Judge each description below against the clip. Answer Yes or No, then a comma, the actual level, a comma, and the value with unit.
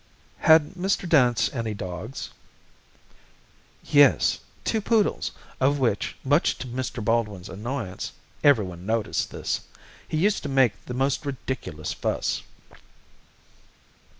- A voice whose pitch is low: Yes, low, 130 Hz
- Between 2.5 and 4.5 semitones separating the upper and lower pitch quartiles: No, average, 5.2 semitones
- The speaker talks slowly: Yes, slow, 110 wpm